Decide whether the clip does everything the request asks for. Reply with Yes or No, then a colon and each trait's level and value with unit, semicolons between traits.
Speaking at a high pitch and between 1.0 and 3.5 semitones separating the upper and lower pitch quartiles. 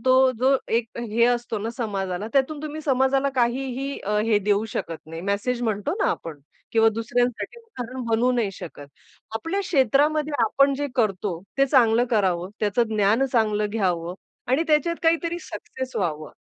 No: high, 235 Hz; average, 4.7 semitones